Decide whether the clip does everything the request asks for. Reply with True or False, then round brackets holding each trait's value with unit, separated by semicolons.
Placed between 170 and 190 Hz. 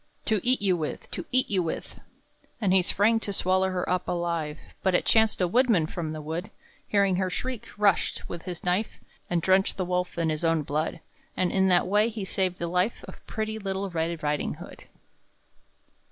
True (185 Hz)